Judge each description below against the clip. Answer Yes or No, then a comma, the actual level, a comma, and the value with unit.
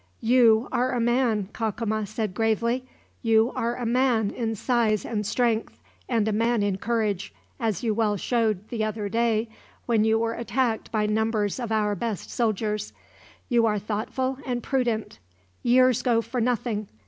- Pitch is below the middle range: No, high, 225 Hz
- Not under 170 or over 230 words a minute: No, average, 160 wpm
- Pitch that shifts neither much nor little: No, narrow, 1.9 semitones